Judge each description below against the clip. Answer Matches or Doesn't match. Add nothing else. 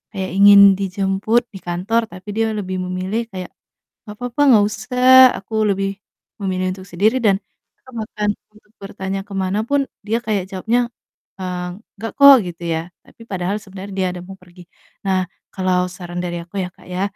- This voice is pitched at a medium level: Doesn't match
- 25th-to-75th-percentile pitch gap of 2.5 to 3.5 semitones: Matches